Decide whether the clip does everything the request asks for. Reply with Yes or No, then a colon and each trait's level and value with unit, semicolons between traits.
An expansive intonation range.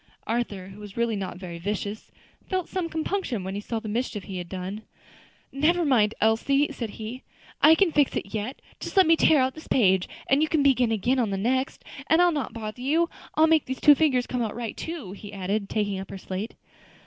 Yes: wide, 6.4 semitones